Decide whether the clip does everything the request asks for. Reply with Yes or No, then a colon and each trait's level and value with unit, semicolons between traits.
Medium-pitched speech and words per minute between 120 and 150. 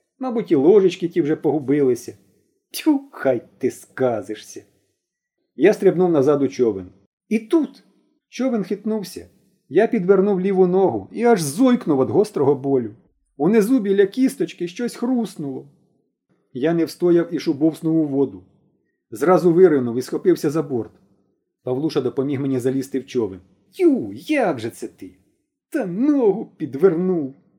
Yes: medium, 180 Hz; average, 135 wpm